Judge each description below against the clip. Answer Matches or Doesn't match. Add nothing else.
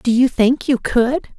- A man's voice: Doesn't match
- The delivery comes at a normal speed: Doesn't match